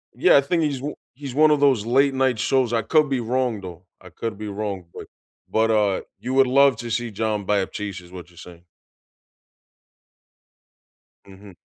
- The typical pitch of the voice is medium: No, low, 115 Hz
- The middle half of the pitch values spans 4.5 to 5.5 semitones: Yes, average, 5.1 semitones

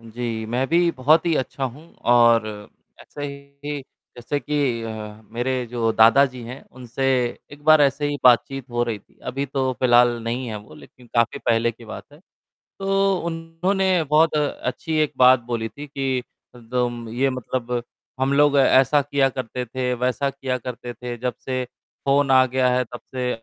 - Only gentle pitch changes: No, average, 3.0 semitones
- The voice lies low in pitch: Yes, low, 130 Hz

